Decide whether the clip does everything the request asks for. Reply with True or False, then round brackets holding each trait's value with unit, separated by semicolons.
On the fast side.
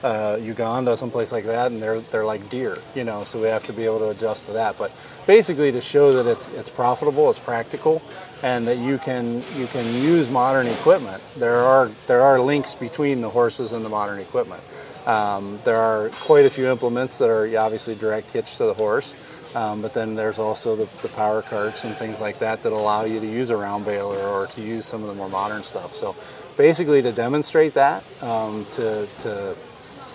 True (210 wpm)